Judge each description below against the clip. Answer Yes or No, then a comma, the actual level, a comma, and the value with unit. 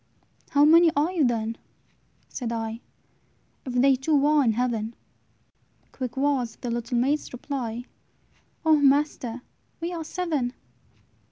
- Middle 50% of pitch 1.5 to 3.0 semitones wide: No, average, 3.9 semitones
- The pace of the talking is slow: Yes, slow, 125 wpm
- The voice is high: Yes, very high, 265 Hz